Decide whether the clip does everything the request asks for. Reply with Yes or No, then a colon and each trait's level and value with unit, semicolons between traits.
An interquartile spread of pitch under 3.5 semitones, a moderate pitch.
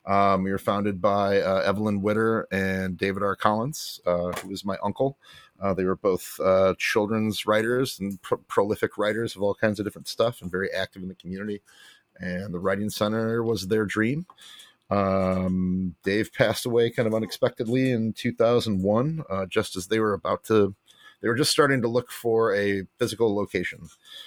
No: average, 3.0 semitones; low, 105 Hz